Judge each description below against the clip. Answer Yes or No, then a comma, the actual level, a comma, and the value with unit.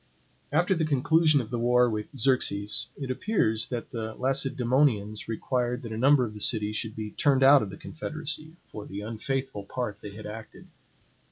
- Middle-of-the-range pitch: No, low, 125 Hz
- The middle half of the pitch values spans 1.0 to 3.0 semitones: No, average, 4.1 semitones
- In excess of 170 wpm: Yes, average, 180 wpm